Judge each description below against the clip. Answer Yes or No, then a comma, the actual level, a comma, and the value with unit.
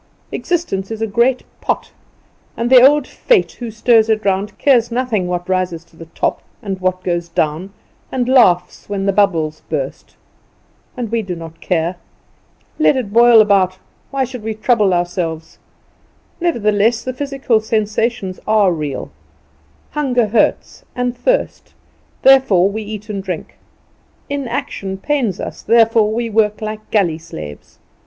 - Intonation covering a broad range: No, average, 4.6 semitones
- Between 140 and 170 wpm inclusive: Yes, average, 145 wpm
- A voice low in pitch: No, high, 215 Hz